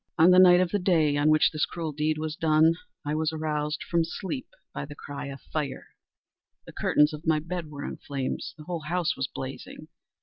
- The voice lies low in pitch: No, medium, 155 Hz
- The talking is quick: Yes, fast, 210 wpm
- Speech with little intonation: Yes, narrow, 2.1 semitones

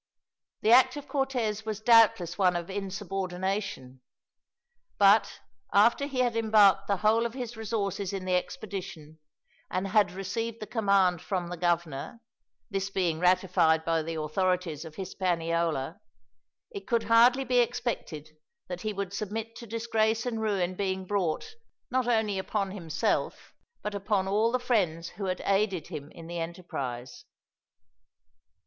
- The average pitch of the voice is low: No, high, 195 Hz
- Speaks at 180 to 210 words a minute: No, average, 145 wpm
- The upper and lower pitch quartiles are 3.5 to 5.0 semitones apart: Yes, average, 4.0 semitones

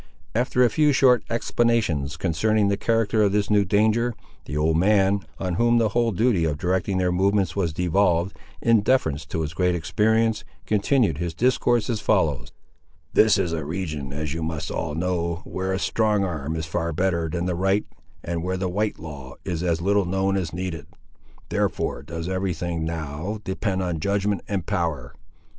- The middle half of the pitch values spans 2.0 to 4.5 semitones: Yes, average, 4.2 semitones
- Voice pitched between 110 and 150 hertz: No, very low, 95 Hz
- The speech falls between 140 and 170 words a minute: No, average, 180 wpm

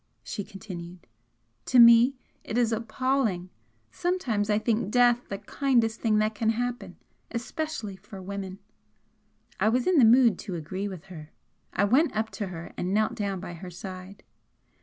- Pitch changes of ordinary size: Yes, average, 4.1 semitones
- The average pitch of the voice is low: No, high, 215 Hz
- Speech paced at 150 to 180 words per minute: Yes, average, 160 wpm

